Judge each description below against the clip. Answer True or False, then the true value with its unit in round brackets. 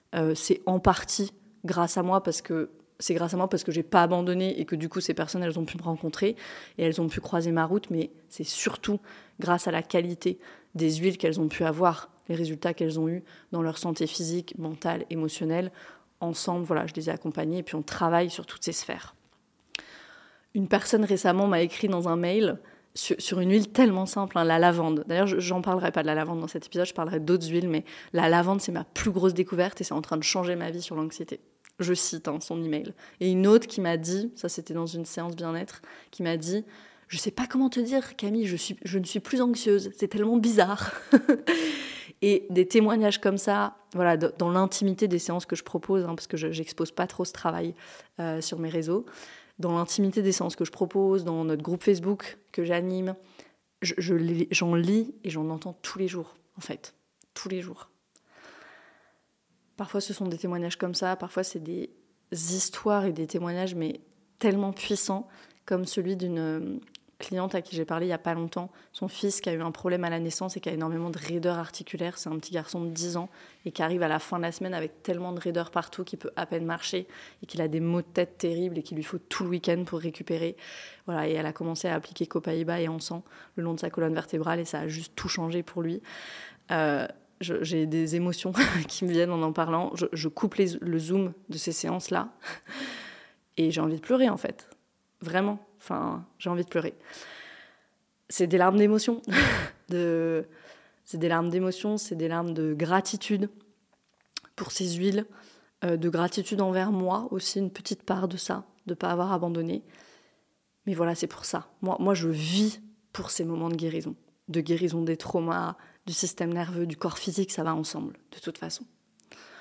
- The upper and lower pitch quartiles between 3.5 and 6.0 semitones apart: False (2.8 semitones)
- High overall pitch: False (175 Hz)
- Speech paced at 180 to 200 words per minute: False (215 wpm)